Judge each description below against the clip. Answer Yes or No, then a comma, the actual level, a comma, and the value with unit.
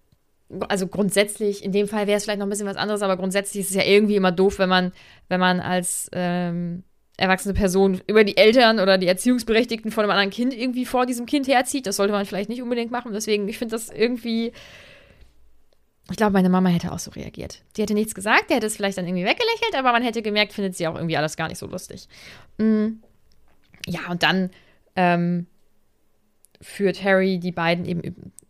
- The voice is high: Yes, high, 195 Hz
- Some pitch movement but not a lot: Yes, average, 3.2 semitones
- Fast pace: Yes, fast, 205 wpm